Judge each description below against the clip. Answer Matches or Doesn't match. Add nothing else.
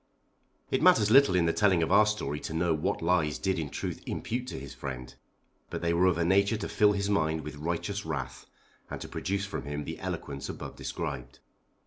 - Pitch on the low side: Matches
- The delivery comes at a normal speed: Doesn't match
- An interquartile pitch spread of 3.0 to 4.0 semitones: Doesn't match